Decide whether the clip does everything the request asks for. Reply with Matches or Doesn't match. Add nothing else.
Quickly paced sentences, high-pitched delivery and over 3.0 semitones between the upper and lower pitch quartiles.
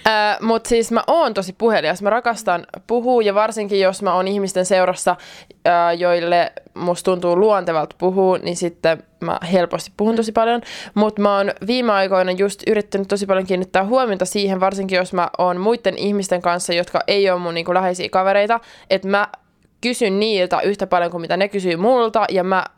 Doesn't match